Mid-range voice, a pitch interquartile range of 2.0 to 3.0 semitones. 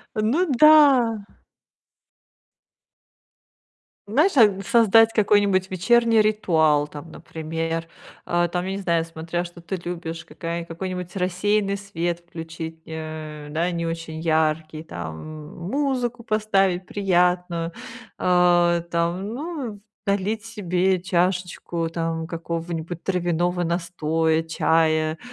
No: medium, 175 Hz; average, 3.4 semitones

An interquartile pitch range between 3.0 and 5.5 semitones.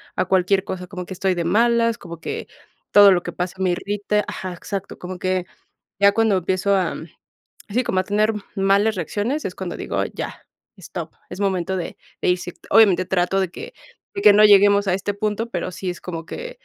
No: narrow, 2.4 semitones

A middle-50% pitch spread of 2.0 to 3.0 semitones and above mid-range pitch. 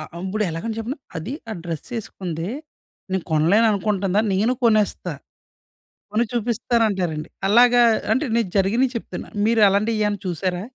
No: average, 3.7 semitones; high, 210 Hz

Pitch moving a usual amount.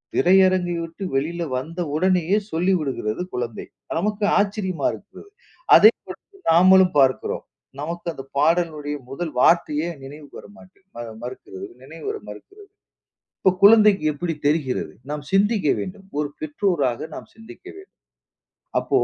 Yes: average, 4.9 semitones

